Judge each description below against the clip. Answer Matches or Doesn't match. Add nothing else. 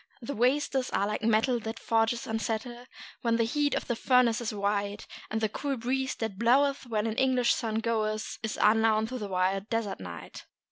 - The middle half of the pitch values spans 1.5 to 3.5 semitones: Matches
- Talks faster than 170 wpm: Matches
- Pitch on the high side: Matches